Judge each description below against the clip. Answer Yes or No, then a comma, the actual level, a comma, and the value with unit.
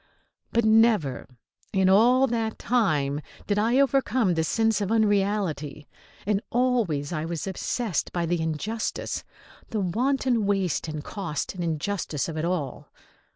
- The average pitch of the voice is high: Yes, high, 200 Hz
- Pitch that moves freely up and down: Yes, wide, 5.9 semitones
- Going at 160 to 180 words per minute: No, average, 140 wpm